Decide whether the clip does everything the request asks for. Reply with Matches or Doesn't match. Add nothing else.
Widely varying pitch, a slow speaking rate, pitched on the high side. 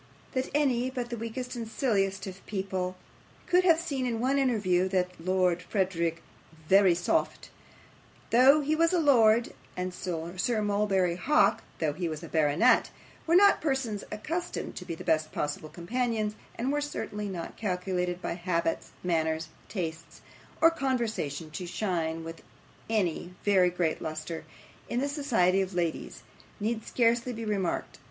Doesn't match